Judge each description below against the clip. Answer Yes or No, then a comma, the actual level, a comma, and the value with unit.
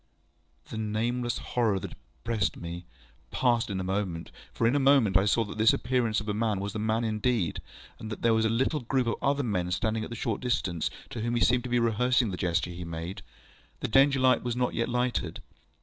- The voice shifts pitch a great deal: No, average, 3.7 semitones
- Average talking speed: No, fast, 225 wpm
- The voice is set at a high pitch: No, low, 110 Hz